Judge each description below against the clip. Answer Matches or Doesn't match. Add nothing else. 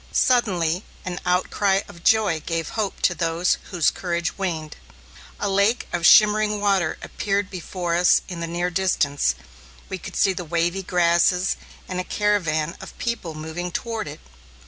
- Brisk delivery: Doesn't match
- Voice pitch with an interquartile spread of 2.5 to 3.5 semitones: Matches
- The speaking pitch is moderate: Matches